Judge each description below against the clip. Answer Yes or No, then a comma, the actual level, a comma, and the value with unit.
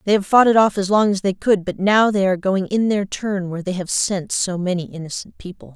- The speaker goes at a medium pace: No, fast, 270 wpm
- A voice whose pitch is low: No, high, 195 Hz